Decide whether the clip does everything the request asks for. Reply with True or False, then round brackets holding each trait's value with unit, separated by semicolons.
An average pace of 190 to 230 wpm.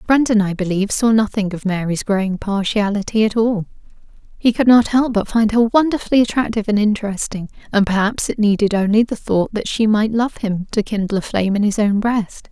True (200 wpm)